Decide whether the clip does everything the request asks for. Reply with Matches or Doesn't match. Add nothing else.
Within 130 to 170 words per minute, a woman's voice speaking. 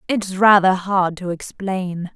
Matches